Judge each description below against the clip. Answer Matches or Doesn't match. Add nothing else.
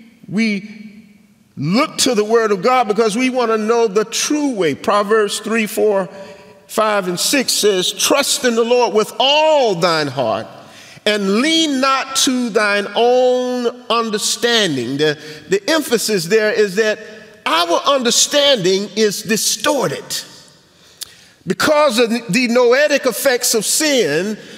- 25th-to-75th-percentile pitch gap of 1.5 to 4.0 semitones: Matches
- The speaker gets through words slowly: Matches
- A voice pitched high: Matches